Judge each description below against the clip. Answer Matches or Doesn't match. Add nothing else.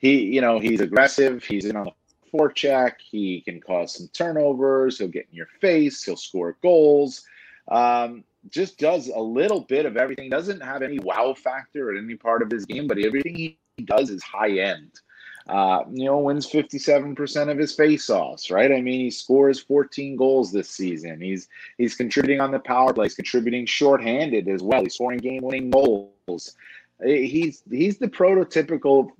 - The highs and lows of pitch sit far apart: Doesn't match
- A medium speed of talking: Matches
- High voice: Doesn't match